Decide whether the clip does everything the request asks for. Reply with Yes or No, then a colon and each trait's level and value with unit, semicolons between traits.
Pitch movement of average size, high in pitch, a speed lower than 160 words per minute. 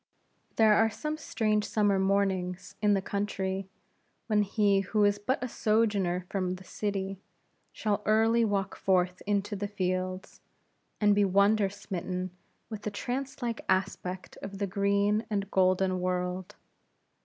No: narrow, 2.1 semitones; high, 200 Hz; average, 145 wpm